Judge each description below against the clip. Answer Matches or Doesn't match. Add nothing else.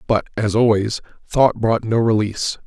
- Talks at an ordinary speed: Matches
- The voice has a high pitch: Doesn't match